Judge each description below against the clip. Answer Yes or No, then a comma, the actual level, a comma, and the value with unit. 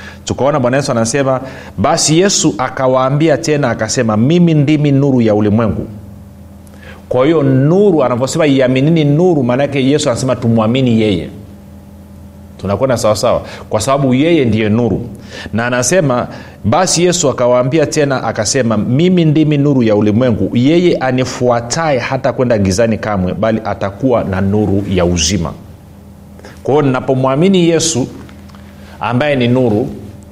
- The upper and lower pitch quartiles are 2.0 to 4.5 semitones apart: No, wide, 5.6 semitones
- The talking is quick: No, average, 125 wpm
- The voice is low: Yes, low, 120 Hz